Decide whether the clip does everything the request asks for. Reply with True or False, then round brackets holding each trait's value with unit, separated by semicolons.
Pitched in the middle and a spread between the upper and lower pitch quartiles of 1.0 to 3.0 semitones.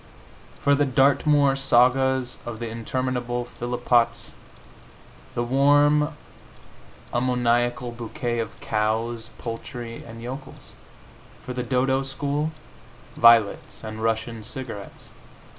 False (120 Hz; 2.5 semitones)